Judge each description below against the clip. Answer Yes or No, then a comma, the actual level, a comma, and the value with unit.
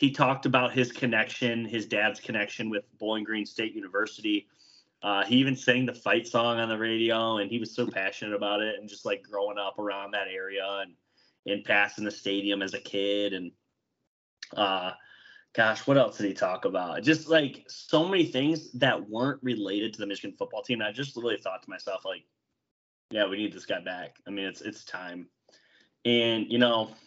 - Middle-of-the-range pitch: No, low, 110 Hz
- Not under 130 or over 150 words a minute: No, average, 200 wpm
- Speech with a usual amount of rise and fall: Yes, average, 3.6 semitones